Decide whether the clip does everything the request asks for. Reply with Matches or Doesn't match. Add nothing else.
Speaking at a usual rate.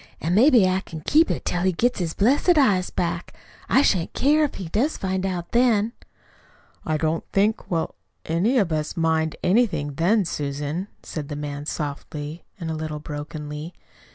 Matches